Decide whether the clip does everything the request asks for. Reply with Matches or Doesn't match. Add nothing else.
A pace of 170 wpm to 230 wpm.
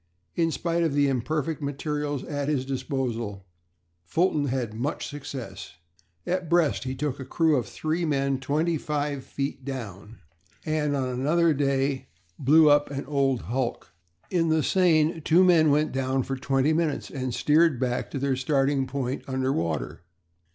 Doesn't match